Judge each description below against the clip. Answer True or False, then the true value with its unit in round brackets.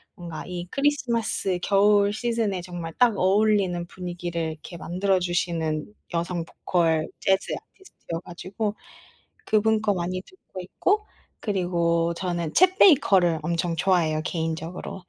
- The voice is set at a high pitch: False (180 Hz)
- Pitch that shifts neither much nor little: True (3.3 semitones)